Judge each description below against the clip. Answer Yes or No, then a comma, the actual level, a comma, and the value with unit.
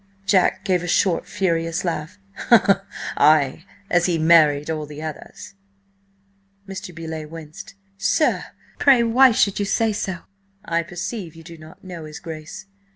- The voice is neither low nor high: Yes, medium, 170 Hz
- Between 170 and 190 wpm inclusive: No, average, 145 wpm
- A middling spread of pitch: Yes, average, 3.3 semitones